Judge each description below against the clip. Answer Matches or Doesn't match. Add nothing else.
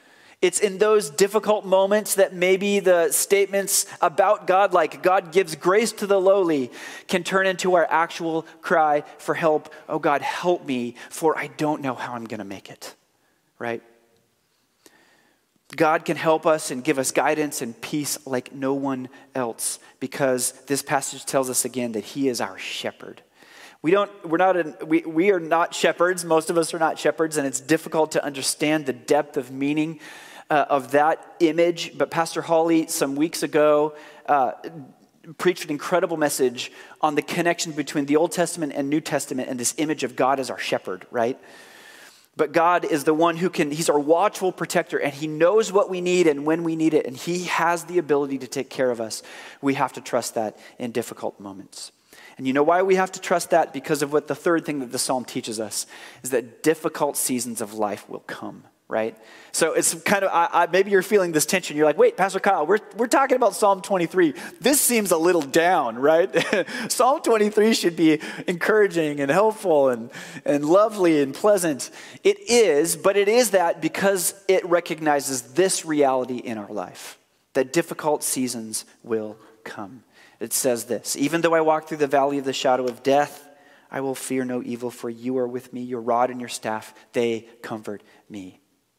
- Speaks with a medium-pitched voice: Matches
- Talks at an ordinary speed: Matches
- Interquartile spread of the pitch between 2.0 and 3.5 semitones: Doesn't match